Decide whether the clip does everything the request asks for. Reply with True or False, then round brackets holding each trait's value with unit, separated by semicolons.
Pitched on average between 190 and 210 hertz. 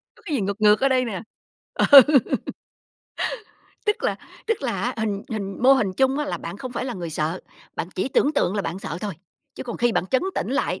False (225 Hz)